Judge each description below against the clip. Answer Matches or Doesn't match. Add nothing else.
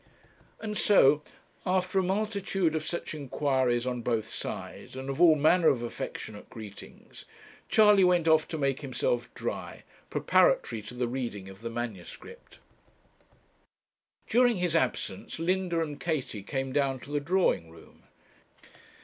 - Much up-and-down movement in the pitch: Matches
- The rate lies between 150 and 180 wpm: Doesn't match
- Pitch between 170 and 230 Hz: Doesn't match